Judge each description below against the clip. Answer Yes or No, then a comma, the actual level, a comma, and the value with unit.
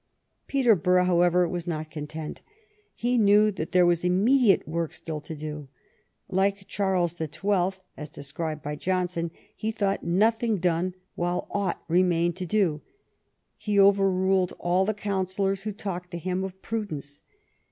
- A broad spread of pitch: No, average, 2.9 semitones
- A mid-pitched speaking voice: Yes, medium, 180 Hz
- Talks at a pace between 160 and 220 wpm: No, average, 145 wpm